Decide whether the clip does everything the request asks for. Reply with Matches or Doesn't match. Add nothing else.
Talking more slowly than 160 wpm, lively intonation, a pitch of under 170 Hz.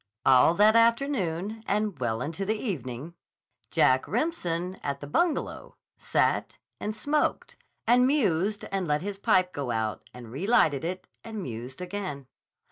Doesn't match